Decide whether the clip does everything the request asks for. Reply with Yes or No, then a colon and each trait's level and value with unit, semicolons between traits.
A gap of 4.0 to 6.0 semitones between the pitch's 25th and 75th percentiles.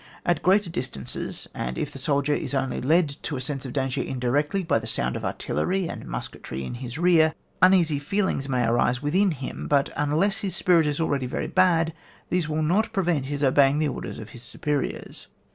Yes: average, 4.6 semitones